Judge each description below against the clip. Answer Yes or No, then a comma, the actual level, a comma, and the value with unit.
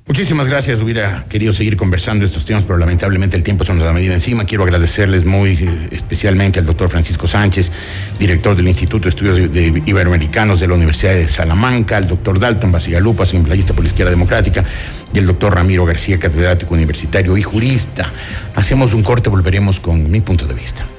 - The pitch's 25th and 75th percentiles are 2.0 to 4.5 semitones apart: Yes, average, 2.8 semitones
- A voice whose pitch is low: Yes, very low, 95 Hz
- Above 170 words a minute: Yes, average, 185 wpm